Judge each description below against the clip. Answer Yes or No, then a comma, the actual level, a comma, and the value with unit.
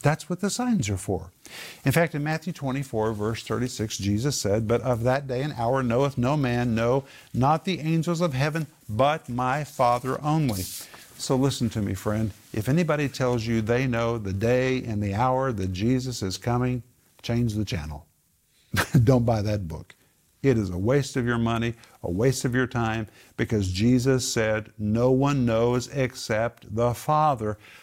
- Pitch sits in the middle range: No, low, 120 Hz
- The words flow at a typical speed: Yes, average, 175 wpm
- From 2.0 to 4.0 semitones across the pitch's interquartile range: Yes, average, 3.6 semitones